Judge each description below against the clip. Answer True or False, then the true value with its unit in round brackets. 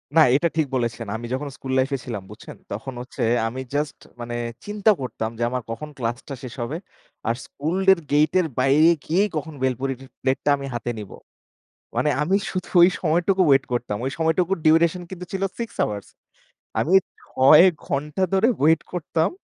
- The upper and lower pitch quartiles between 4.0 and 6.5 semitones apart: True (5.1 semitones)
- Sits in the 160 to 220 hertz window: False (145 Hz)